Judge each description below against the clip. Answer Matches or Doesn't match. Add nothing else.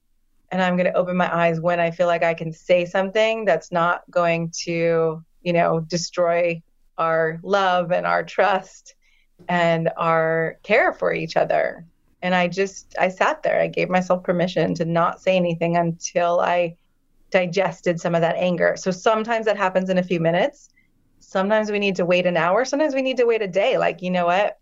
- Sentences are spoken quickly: Doesn't match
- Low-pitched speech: Doesn't match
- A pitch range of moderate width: Doesn't match